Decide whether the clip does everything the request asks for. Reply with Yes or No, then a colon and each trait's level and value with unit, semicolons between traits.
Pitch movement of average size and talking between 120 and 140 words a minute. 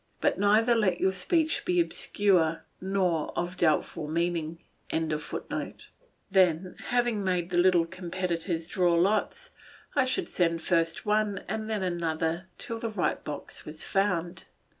Yes: average, 3.7 semitones; slow, 135 wpm